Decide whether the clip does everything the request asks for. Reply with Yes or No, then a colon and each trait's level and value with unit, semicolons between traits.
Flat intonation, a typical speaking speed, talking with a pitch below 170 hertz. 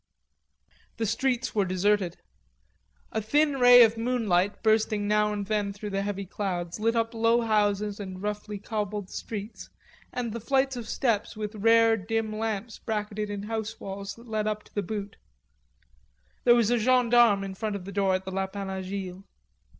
No: narrow, 2.3 semitones; average, 175 wpm; high, 210 Hz